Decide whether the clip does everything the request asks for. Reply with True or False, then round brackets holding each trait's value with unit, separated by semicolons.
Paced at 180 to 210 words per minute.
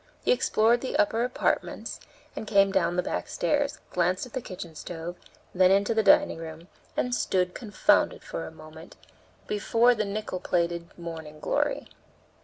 False (160 wpm)